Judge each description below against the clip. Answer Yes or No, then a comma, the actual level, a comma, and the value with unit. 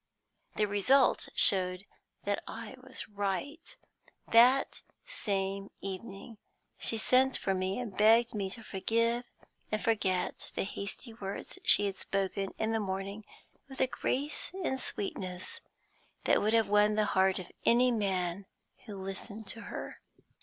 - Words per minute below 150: Yes, average, 140 wpm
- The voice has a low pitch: No, high, 205 Hz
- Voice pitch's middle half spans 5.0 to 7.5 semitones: No, average, 3.1 semitones